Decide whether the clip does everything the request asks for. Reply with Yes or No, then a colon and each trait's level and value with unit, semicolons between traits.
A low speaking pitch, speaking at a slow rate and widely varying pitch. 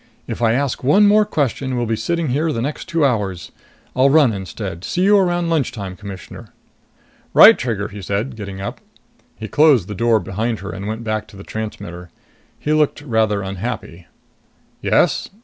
No: low, 115 Hz; average, 175 wpm; wide, 6.4 semitones